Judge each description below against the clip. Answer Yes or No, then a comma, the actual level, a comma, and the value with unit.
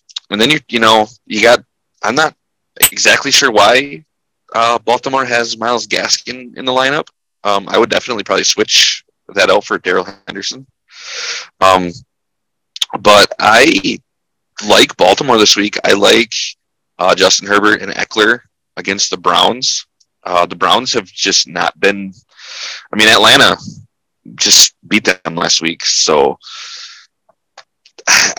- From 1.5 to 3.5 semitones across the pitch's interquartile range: No, average, 4.5 semitones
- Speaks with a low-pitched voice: Yes, low, 110 Hz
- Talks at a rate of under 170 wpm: Yes, slow, 135 wpm